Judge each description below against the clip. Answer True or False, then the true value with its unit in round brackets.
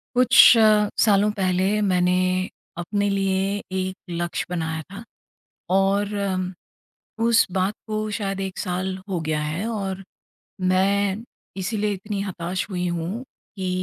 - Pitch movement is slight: True (2.0 semitones)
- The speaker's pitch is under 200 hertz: True (190 Hz)